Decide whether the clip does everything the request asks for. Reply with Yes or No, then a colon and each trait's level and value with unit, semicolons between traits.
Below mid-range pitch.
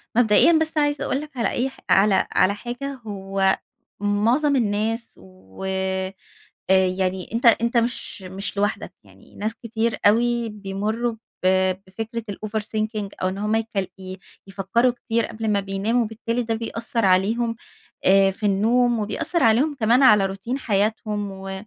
No: high, 215 Hz